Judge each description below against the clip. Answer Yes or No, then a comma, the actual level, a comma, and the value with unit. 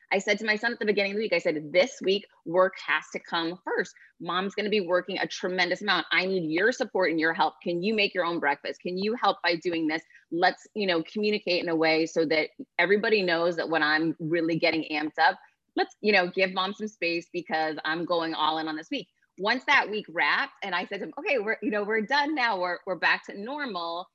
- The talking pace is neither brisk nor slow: No, fast, 250 wpm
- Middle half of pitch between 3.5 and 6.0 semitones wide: Yes, average, 4.0 semitones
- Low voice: No, medium, 180 Hz